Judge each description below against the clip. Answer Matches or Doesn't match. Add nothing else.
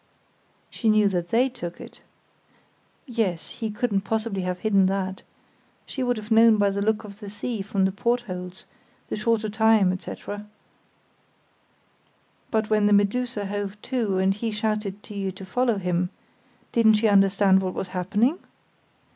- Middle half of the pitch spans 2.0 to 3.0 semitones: Matches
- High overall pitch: Matches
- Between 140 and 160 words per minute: Matches